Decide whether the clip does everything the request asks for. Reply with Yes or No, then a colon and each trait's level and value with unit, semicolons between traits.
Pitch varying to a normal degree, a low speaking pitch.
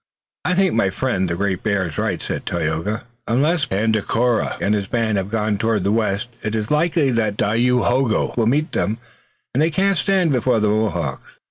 Yes: average, 4.4 semitones; low, 110 Hz